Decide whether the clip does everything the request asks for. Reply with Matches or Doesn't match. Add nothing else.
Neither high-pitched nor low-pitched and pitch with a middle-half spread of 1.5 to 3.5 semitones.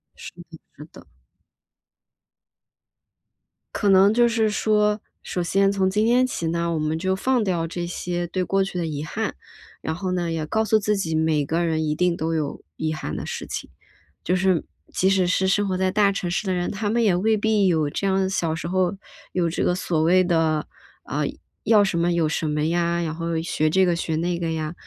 Matches